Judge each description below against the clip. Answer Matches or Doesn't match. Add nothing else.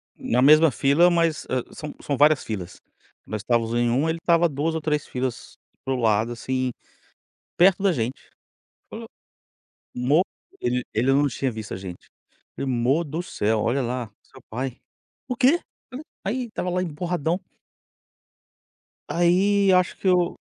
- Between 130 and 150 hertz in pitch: Matches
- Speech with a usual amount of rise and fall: Doesn't match